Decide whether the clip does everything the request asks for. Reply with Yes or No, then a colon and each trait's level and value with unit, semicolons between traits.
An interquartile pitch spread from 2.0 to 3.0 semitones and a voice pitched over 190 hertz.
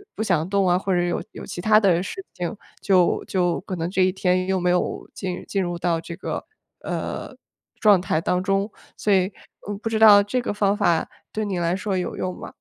No: narrow, 2.4 semitones; medium, 185 Hz